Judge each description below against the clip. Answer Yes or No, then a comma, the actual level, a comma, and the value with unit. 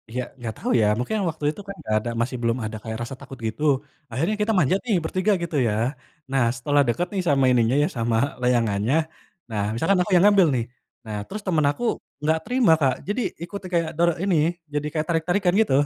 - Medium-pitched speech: Yes, medium, 150 Hz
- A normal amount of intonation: No, wide, 7.6 semitones